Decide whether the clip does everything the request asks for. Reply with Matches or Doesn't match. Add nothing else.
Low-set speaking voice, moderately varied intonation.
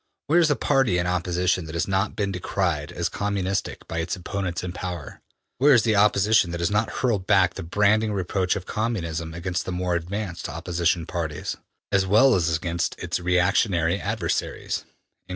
Matches